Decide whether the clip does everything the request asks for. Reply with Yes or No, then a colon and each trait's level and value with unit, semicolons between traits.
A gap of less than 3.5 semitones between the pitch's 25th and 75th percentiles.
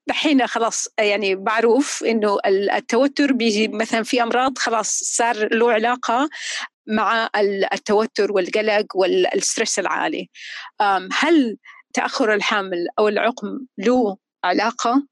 Yes: average, 2.9 semitones